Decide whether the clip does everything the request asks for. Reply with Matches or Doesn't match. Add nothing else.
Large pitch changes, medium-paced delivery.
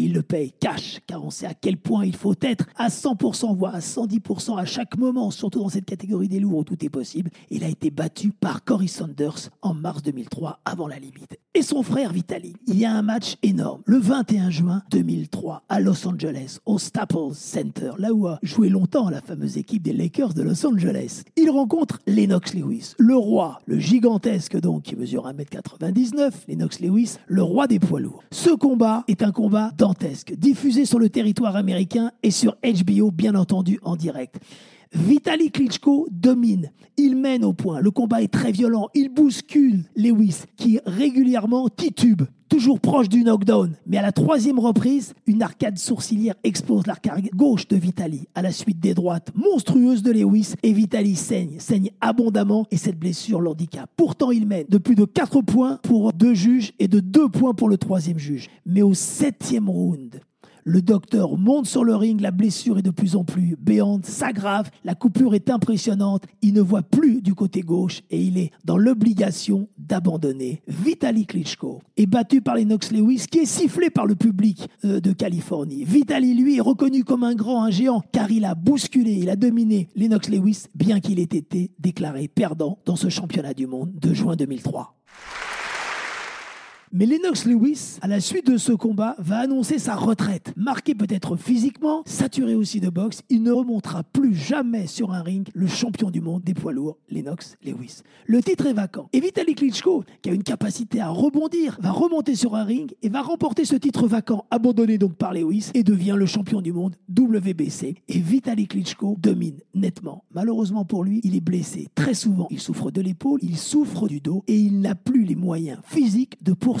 Doesn't match